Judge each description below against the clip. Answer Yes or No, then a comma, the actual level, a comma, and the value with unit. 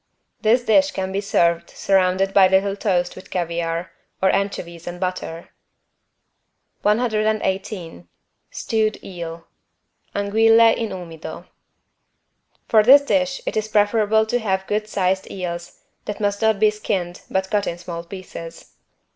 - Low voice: No, high, 195 Hz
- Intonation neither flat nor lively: Yes, average, 3.4 semitones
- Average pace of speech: No, slow, 130 wpm